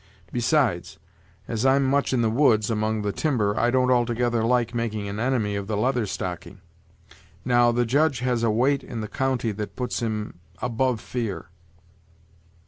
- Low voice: Yes, low, 120 Hz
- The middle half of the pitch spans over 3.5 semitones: No, average, 2.9 semitones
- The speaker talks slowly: No, average, 165 wpm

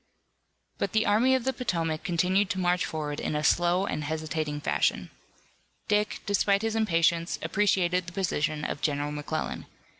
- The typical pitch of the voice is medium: Yes, medium, 175 Hz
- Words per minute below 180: Yes, average, 155 wpm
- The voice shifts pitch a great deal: No, average, 4.5 semitones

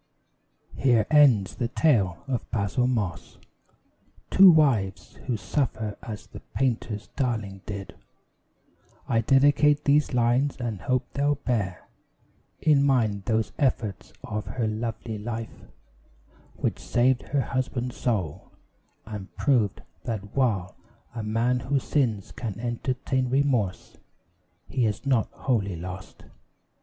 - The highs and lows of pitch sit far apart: No, average, 4.1 semitones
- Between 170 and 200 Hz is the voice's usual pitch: No, low, 115 Hz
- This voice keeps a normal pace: No, slow, 120 wpm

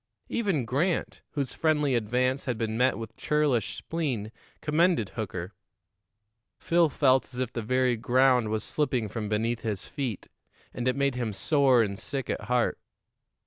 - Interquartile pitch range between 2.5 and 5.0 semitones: Yes, average, 4.0 semitones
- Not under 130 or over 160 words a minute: Yes, average, 155 wpm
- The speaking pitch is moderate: No, low, 125 Hz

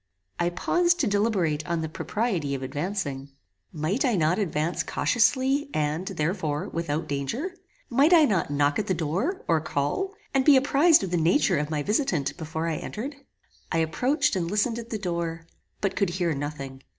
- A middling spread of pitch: No, wide, 7.4 semitones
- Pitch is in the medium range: Yes, medium, 175 Hz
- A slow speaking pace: No, average, 175 wpm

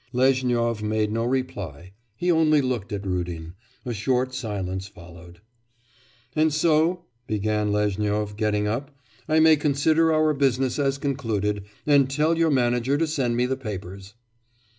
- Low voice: Yes, low, 120 Hz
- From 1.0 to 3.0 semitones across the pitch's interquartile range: No, wide, 5.5 semitones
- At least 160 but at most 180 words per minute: No, average, 140 wpm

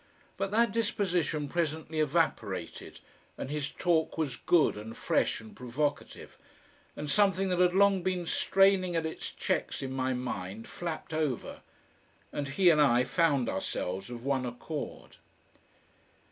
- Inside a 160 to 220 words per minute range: No, average, 140 wpm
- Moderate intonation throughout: No, wide, 5.7 semitones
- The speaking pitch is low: No, medium, 155 Hz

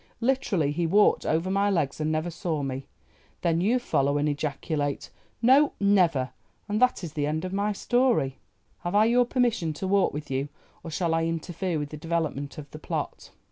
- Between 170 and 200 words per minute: Yes, average, 185 wpm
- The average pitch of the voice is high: No, medium, 165 Hz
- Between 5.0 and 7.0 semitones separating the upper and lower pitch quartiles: Yes, average, 5.3 semitones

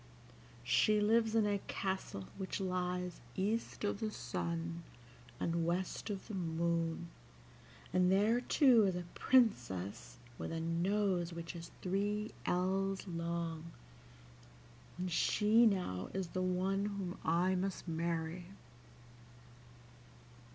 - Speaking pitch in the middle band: Yes, medium, 180 Hz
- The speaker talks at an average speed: No, slow, 115 wpm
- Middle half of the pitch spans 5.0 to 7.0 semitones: No, average, 3.2 semitones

